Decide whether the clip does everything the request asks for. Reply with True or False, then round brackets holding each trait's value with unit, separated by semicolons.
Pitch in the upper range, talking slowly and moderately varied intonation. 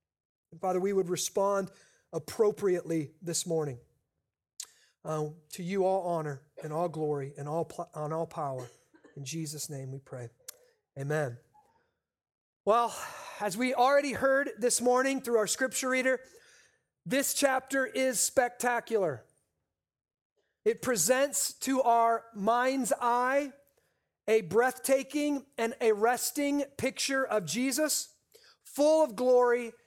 False (235 Hz; 120 wpm; 8.2 semitones)